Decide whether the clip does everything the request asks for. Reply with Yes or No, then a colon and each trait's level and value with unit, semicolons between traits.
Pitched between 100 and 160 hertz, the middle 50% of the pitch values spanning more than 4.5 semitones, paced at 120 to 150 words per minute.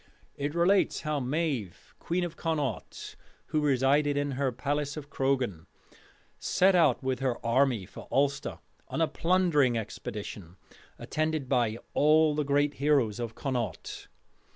No: medium, 140 Hz; average, 3.6 semitones; slow, 135 wpm